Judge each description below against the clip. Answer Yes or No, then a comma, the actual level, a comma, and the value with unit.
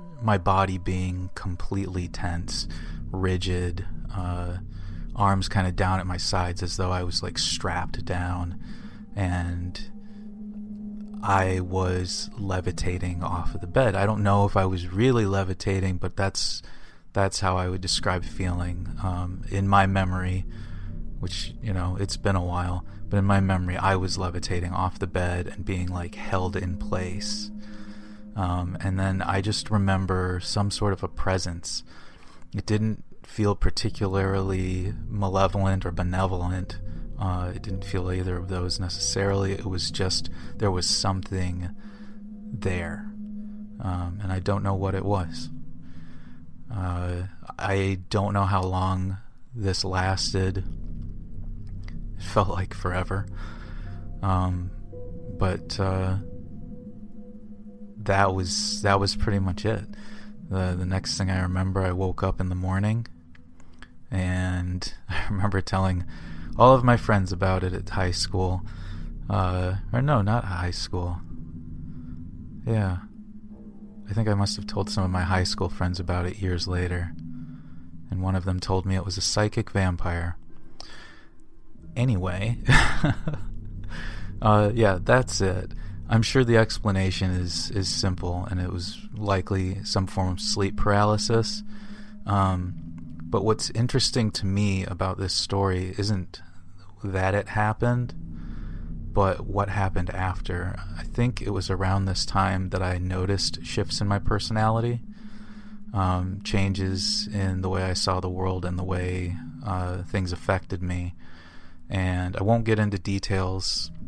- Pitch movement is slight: Yes, narrow, 2.3 semitones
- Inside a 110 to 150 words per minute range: Yes, average, 140 wpm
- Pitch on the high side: No, very low, 95 Hz